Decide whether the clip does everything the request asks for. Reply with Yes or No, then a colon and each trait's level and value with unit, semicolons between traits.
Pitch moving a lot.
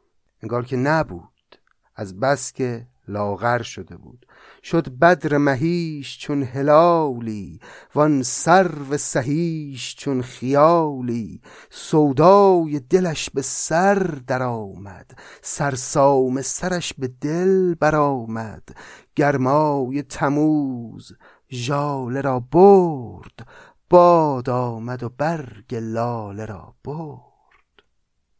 No: average, 4.1 semitones